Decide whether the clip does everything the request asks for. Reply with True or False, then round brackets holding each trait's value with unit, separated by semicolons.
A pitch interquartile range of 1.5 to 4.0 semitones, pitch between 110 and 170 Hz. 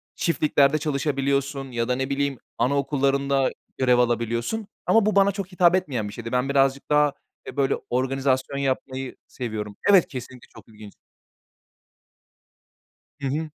True (2.7 semitones; 135 Hz)